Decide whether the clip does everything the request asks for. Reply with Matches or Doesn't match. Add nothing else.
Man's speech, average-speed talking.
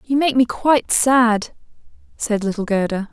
Doesn't match